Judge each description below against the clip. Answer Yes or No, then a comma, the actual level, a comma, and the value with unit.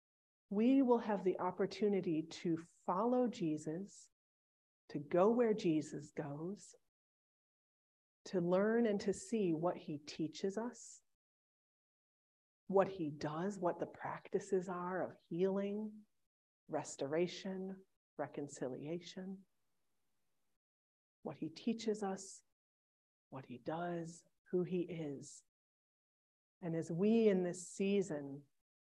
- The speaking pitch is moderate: Yes, medium, 180 Hz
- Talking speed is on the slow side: Yes, slow, 100 wpm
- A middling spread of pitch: Yes, average, 4.3 semitones